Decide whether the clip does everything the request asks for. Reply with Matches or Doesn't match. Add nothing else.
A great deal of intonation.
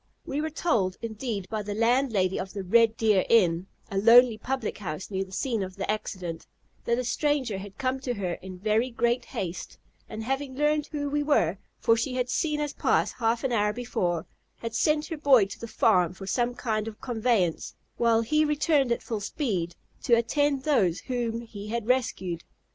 Doesn't match